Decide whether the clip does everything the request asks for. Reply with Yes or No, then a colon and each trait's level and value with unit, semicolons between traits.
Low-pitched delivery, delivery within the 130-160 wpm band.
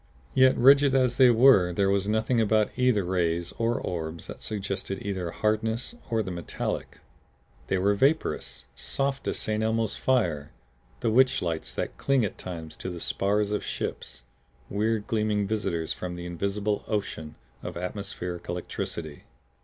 Yes: low, 100 Hz; average, 155 wpm